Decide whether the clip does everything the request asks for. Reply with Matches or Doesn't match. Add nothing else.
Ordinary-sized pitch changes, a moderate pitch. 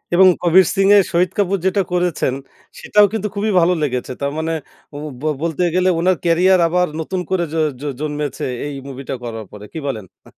Matches